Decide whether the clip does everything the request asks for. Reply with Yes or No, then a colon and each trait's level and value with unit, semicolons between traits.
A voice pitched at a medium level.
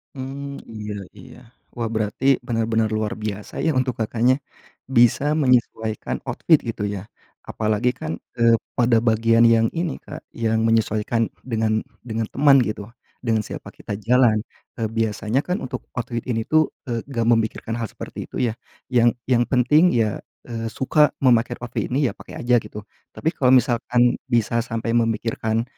No: low, 115 Hz